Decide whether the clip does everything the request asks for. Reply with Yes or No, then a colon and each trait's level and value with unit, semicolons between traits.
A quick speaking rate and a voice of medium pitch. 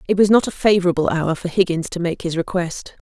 Yes: fast, 235 wpm; medium, 175 Hz